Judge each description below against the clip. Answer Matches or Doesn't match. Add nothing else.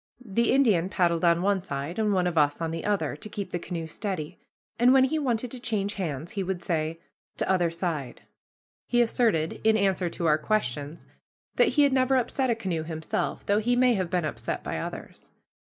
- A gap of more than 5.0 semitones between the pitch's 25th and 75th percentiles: Matches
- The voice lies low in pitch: Doesn't match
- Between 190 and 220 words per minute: Matches